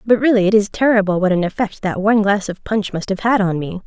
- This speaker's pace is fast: Yes, fast, 280 wpm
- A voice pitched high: Yes, high, 205 Hz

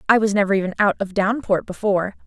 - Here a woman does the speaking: Yes, female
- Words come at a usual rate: No, fast, 210 wpm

